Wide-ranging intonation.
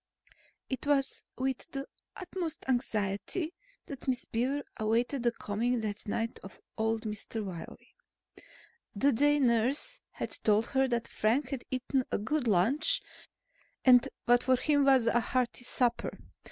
No: average, 3.5 semitones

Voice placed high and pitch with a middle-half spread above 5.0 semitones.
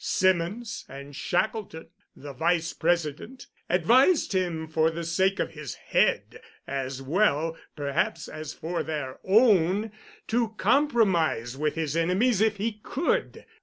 No: medium, 170 Hz; wide, 5.6 semitones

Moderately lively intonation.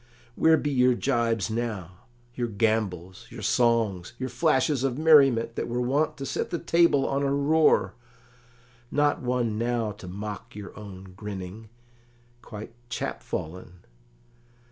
Yes: average, 4.6 semitones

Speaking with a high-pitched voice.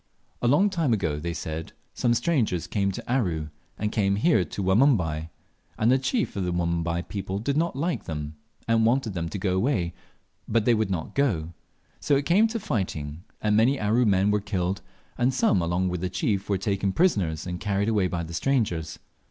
No: low, 100 Hz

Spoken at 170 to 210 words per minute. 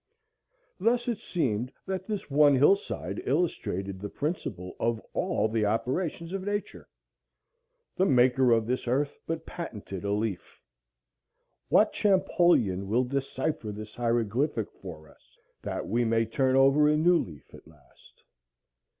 No: slow, 135 wpm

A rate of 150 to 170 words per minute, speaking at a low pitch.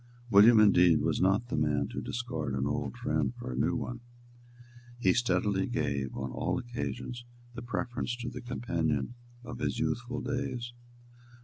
Yes: average, 155 wpm; low, 110 Hz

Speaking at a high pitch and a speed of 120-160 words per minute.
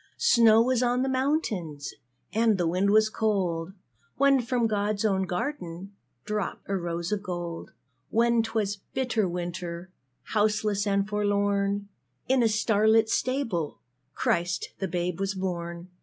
Yes: high, 205 Hz; average, 140 wpm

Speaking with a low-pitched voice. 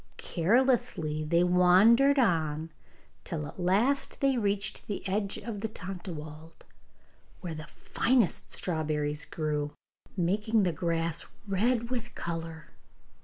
No: medium, 180 Hz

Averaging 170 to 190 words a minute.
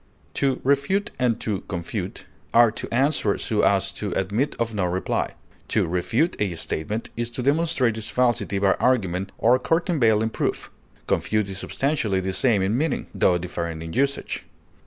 No: average, 160 wpm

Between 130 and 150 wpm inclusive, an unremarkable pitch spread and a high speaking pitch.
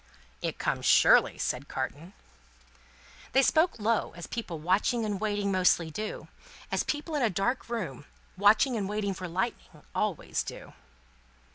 Yes: average, 145 wpm; average, 4.5 semitones; high, 205 Hz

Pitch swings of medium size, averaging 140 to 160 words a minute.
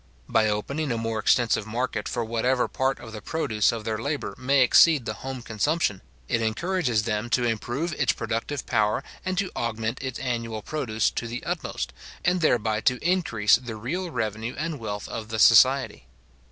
No: average, 3.6 semitones; average, 180 wpm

